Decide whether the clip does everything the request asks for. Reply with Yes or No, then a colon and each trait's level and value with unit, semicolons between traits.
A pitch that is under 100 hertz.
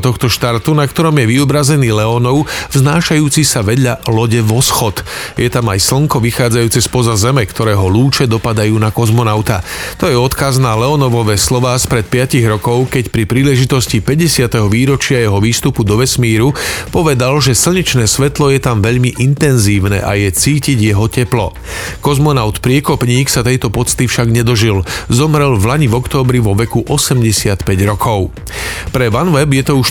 No: low, 125 Hz